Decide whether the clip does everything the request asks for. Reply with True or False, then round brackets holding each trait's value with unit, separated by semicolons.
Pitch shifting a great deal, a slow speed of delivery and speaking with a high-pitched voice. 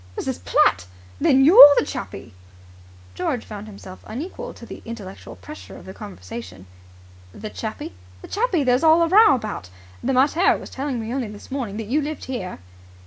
False (6.4 semitones; 175 wpm; 245 Hz)